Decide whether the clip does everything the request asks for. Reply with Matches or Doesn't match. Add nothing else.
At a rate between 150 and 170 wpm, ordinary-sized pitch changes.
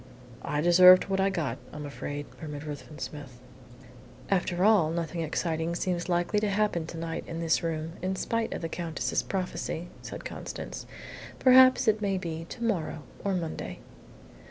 Matches